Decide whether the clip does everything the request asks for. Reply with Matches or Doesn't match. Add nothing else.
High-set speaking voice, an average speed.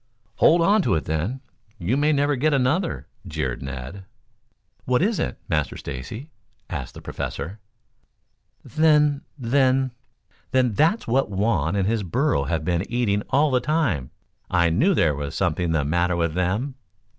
Doesn't match